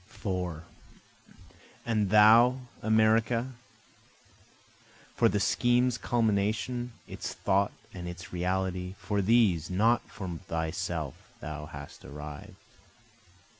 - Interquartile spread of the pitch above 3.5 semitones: Yes, average, 4.5 semitones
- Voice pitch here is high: No, low, 100 Hz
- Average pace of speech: No, slow, 95 wpm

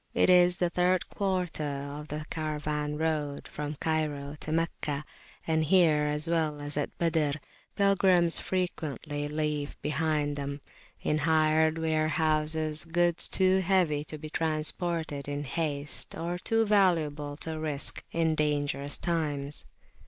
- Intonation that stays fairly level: Yes, narrow, 2.2 semitones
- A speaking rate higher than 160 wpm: No, slow, 135 wpm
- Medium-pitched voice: Yes, medium, 155 Hz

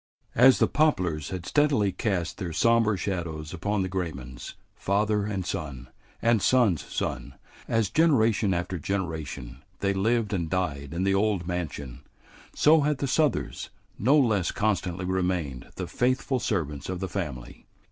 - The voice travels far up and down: No, average, 4.8 semitones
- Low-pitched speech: Yes, very low, 95 Hz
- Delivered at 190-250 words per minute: No, average, 145 wpm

